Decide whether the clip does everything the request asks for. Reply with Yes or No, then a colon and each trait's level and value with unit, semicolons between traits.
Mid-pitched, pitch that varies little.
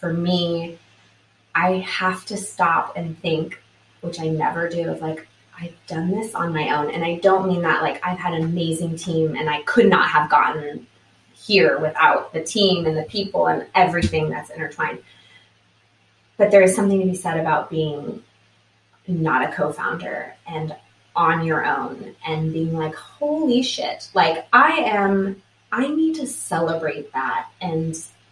No: medium, 165 Hz; average, 3.5 semitones